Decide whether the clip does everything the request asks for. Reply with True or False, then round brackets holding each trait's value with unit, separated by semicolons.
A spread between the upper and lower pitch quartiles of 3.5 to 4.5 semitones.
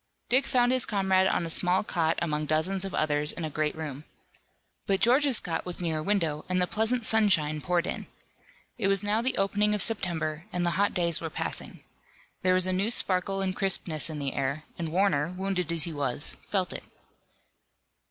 True (4.0 semitones)